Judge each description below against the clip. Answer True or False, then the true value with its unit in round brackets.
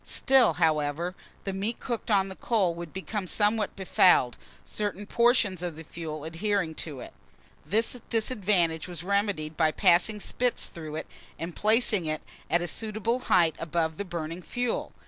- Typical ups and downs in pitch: True (4.7 semitones)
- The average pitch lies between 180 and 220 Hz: True (185 Hz)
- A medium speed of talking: True (160 wpm)